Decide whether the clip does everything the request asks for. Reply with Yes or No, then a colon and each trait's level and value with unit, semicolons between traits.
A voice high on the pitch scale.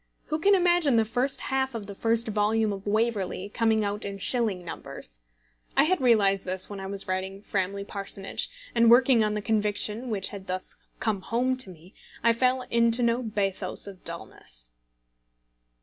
Yes: high, 210 Hz